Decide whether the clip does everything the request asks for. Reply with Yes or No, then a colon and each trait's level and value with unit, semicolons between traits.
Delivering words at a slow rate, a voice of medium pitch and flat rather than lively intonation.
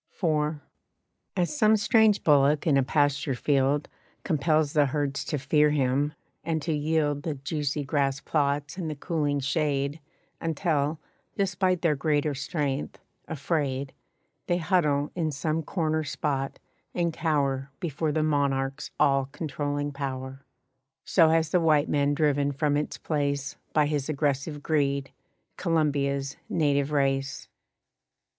Yes: slow, 130 wpm; medium, 145 Hz; narrow, 2.2 semitones